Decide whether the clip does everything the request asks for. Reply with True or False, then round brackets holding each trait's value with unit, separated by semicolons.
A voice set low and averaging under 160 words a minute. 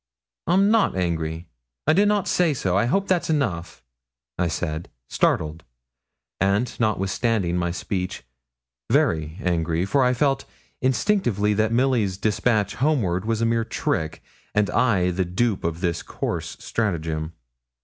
True (100 Hz; 140 wpm)